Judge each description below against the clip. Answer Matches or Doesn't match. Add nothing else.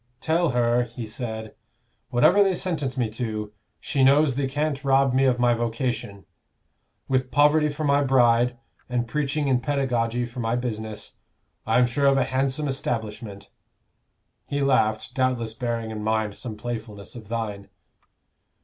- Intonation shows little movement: Doesn't match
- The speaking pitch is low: Matches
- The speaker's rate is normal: Matches